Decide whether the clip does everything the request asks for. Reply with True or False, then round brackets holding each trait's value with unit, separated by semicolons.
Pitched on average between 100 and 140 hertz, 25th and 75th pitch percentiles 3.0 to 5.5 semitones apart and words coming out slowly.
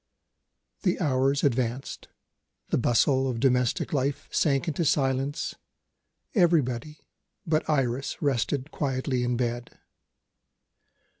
False (135 Hz; 2.6 semitones; 95 wpm)